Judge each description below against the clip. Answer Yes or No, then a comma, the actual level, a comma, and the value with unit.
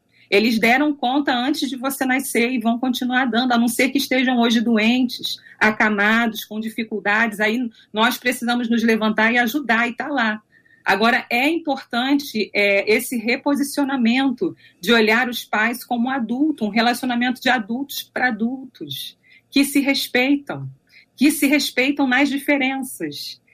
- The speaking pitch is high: Yes, high, 245 Hz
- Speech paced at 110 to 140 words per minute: No, average, 150 wpm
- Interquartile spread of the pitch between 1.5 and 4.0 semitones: Yes, average, 3.0 semitones